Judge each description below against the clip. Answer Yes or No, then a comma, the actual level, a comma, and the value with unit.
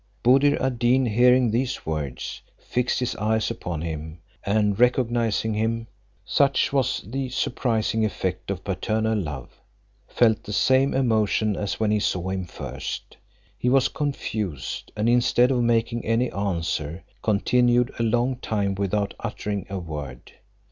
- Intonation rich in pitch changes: No, average, 3.8 semitones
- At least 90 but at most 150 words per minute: Yes, average, 140 wpm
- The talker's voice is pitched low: Yes, low, 110 Hz